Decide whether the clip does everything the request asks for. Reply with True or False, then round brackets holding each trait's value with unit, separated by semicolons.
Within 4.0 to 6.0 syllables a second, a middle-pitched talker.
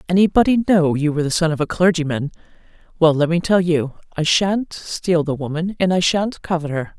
True (5.4 syllables/s; 170 Hz)